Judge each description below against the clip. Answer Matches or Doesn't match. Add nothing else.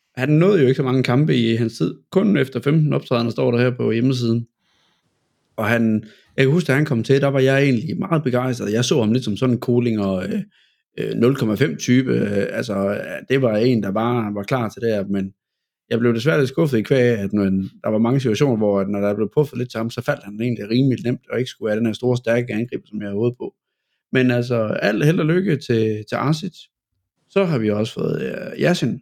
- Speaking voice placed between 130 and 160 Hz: Doesn't match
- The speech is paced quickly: Matches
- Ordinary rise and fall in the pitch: Matches